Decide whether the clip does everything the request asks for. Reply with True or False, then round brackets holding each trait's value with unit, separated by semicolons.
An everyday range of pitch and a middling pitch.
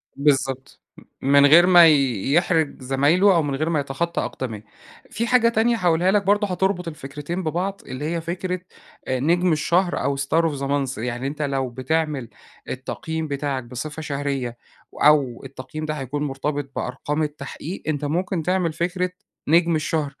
True (4.0 semitones; 150 Hz)